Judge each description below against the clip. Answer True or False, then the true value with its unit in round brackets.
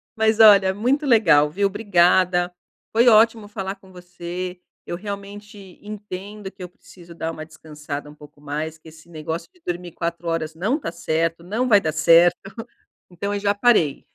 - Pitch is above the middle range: False (180 Hz)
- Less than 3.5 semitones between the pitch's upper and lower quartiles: False (3.8 semitones)